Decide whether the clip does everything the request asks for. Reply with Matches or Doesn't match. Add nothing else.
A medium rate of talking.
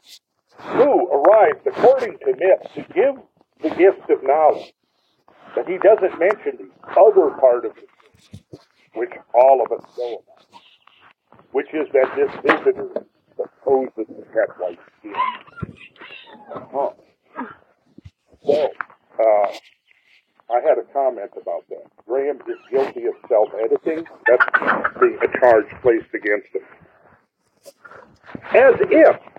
Doesn't match